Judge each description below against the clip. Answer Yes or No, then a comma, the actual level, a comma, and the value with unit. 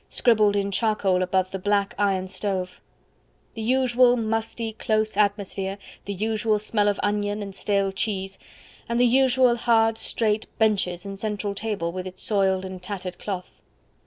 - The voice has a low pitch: No, high, 205 Hz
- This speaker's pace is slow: No, average, 150 wpm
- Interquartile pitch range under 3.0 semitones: Yes, narrow, 2.5 semitones